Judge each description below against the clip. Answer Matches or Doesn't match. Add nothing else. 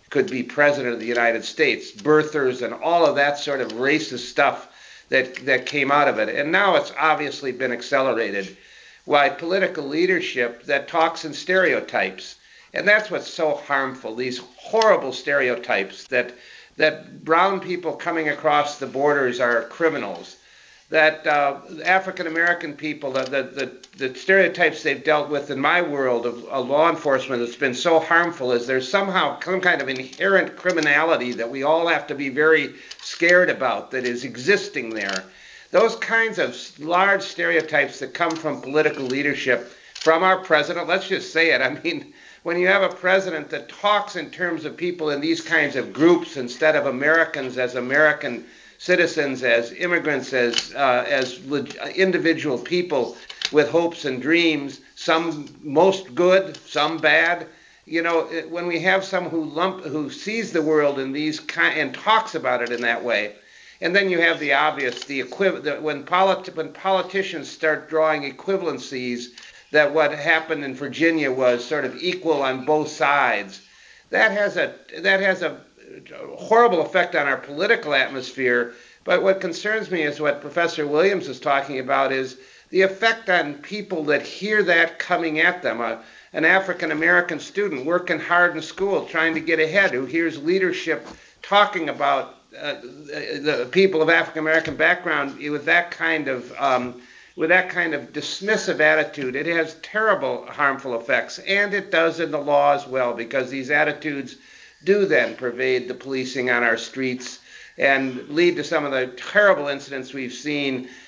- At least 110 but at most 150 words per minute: Doesn't match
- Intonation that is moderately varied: Matches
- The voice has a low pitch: Doesn't match